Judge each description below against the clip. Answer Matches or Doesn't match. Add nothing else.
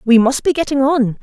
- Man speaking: Doesn't match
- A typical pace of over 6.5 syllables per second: Doesn't match